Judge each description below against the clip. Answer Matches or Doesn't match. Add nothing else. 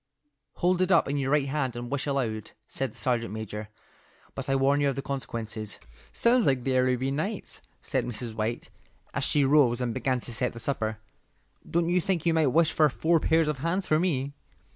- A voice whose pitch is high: Doesn't match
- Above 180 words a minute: Matches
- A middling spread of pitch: Matches